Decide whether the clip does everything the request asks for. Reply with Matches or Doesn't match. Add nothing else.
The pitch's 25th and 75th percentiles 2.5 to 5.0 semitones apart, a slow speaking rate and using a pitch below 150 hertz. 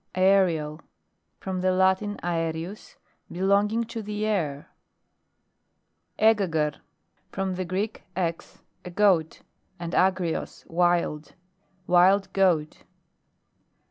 Doesn't match